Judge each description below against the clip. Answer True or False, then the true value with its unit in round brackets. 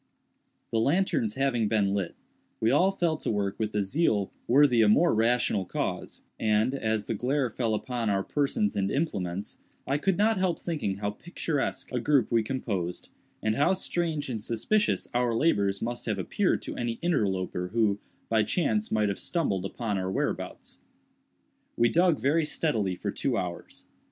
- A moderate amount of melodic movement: False (6.2 semitones)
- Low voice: True (115 Hz)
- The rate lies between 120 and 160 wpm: False (170 wpm)